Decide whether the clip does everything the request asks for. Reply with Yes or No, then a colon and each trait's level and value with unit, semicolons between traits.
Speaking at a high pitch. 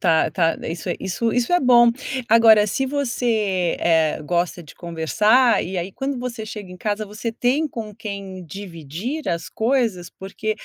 Yes: high, 205 Hz